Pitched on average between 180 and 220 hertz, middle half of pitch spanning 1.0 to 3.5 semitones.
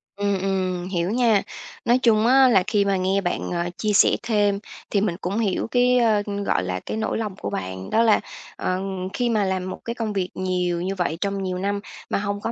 Yes: high, 200 Hz; average, 3.0 semitones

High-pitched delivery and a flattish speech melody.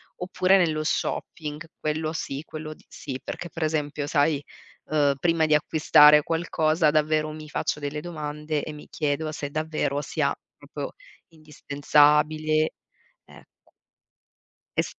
No: medium, 155 Hz; narrow, 1.0 semitones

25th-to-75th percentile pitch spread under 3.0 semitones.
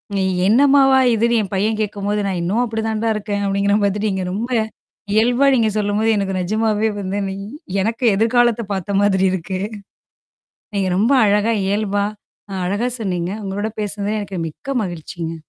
Yes: narrow, 2.4 semitones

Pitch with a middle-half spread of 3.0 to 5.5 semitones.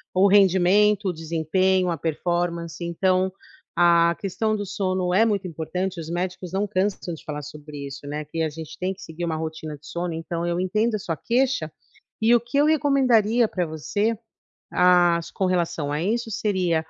Yes: average, 3.7 semitones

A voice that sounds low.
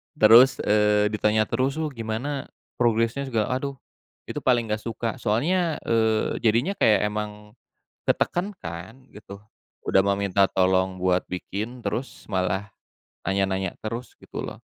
Yes: low, 110 Hz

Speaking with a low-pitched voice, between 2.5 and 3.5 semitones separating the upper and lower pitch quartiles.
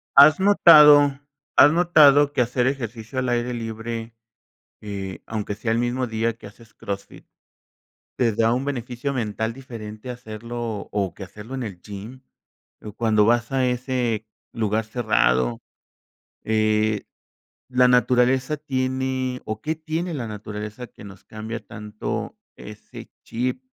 Yes: low, 120 Hz; average, 3.2 semitones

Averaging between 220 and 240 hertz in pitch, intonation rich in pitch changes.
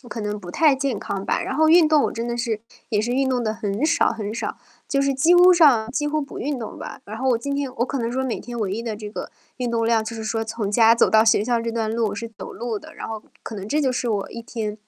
No: high, 235 Hz; average, 3.3 semitones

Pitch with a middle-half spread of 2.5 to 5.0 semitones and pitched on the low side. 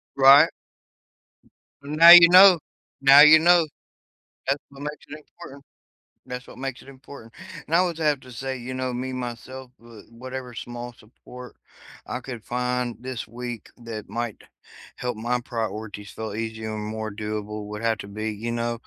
Yes: average, 3.4 semitones; low, 125 Hz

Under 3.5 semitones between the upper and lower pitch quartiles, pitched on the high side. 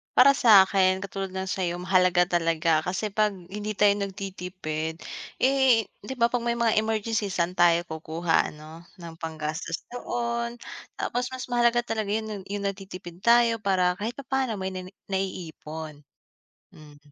No: average, 4.5 semitones; high, 195 Hz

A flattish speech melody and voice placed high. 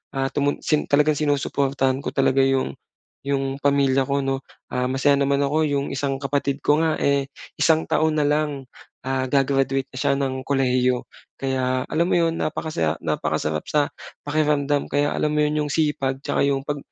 No: narrow, 1.6 semitones; medium, 140 Hz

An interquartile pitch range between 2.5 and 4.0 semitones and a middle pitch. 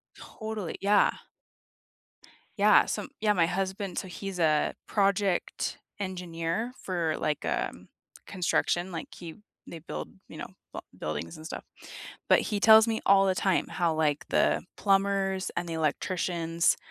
Yes: average, 3.1 semitones; medium, 180 Hz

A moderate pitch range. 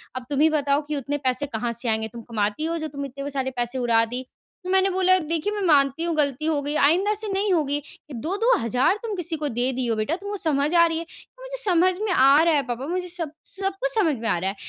No: wide, 5.8 semitones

